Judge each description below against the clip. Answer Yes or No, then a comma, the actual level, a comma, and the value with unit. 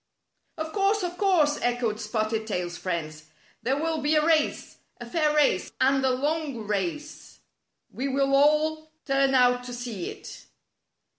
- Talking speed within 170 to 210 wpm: No, average, 160 wpm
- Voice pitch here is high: Yes, very high, 275 Hz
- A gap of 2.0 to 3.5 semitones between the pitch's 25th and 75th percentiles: No, average, 5.1 semitones